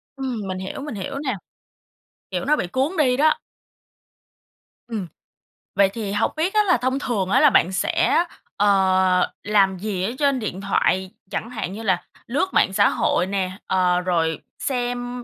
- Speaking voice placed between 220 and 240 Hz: No, high, 210 Hz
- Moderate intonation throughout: No, wide, 5.8 semitones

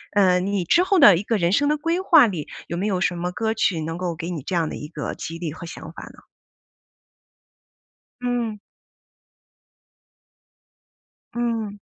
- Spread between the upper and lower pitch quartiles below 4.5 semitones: No, wide, 5.4 semitones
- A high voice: Yes, high, 195 Hz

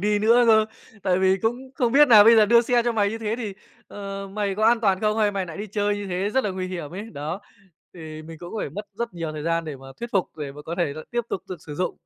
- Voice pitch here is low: No, high, 200 Hz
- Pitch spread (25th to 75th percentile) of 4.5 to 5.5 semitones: No, average, 4.1 semitones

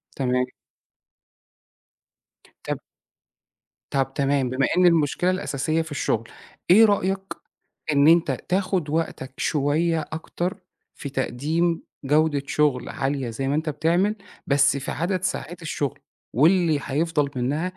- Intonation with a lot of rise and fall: No, average, 3.8 semitones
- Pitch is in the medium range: Yes, medium, 150 Hz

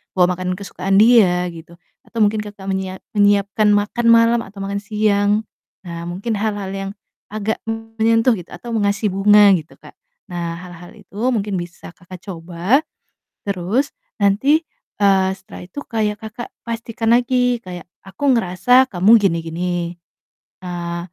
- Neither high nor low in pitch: No, high, 200 Hz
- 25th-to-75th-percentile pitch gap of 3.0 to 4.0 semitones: Yes, average, 3.6 semitones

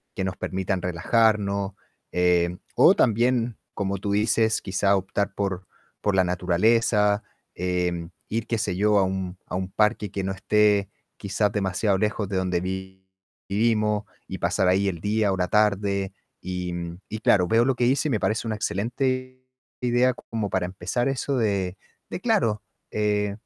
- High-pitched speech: No, low, 100 Hz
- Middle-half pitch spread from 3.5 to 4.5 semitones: No, average, 2.8 semitones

